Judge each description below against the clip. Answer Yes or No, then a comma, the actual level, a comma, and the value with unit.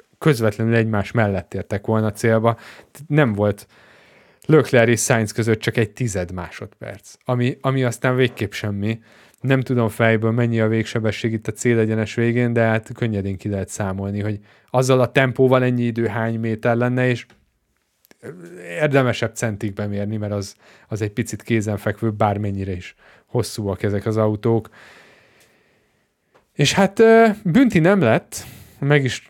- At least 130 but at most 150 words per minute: Yes, average, 140 wpm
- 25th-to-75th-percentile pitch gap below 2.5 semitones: No, average, 2.9 semitones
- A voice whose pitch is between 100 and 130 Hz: Yes, low, 115 Hz